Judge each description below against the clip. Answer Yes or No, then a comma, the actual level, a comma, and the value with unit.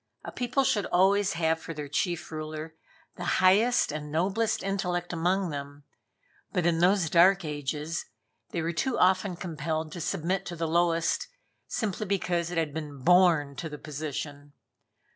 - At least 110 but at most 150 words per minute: No, average, 160 wpm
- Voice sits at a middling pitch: Yes, medium, 170 Hz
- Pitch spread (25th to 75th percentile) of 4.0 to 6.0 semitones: No, average, 3.2 semitones